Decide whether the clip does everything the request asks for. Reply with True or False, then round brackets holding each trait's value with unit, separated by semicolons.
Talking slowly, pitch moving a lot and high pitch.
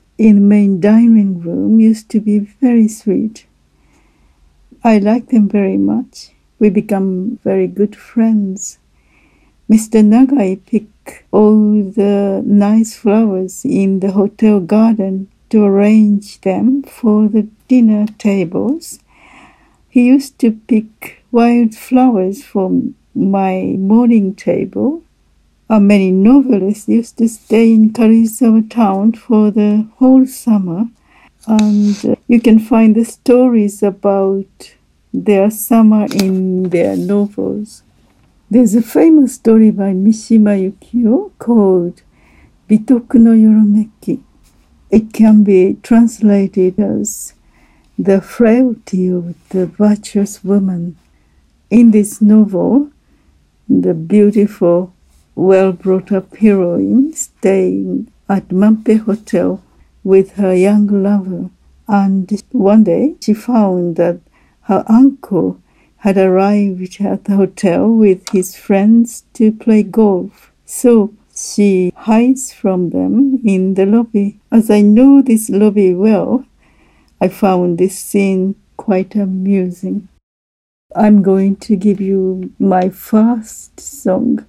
False (115 wpm; 2.8 semitones; 210 Hz)